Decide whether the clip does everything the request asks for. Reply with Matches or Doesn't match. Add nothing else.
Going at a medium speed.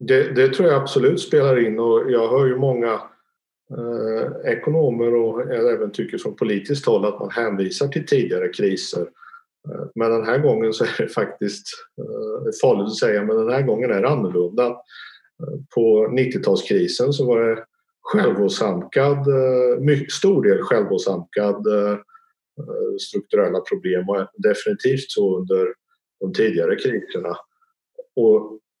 Matches